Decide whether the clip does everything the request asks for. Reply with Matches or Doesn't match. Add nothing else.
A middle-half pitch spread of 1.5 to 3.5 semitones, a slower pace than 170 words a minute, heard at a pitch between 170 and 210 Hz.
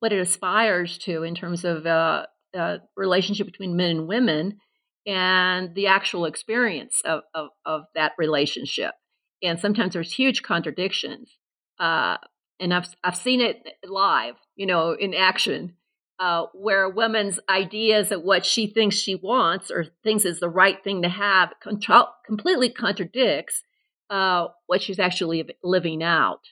Matches